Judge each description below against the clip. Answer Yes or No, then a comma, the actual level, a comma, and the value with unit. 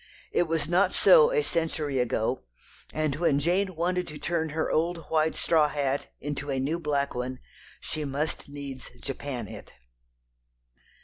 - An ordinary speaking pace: Yes, average, 150 wpm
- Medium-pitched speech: Yes, medium, 150 Hz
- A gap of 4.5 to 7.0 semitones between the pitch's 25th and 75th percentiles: No, average, 3.3 semitones